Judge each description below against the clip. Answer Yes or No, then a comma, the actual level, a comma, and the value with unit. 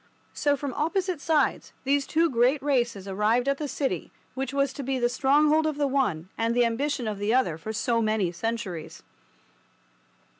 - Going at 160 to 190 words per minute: Yes, average, 180 wpm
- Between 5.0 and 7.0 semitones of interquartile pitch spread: No, average, 4.3 semitones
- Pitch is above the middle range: Yes, very high, 260 Hz